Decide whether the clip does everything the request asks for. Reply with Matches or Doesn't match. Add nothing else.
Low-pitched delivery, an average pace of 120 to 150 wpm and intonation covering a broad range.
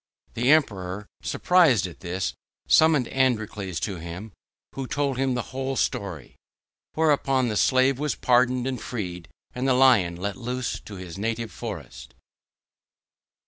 Matches